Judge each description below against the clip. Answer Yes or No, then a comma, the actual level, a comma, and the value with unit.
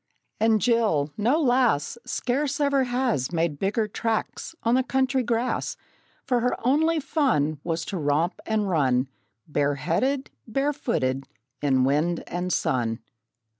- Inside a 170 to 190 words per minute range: No, slow, 135 wpm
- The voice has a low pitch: No, high, 215 Hz